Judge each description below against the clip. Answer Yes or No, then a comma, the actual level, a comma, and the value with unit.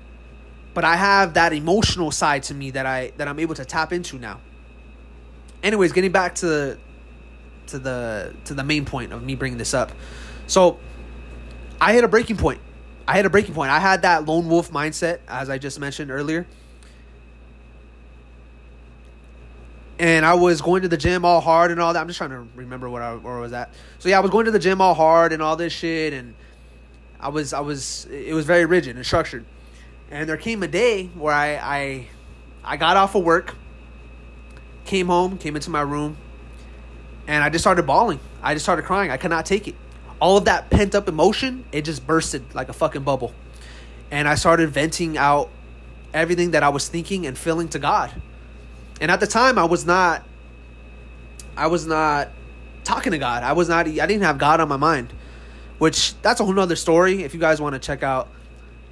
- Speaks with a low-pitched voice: No, medium, 145 Hz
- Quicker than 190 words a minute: Yes, fast, 205 wpm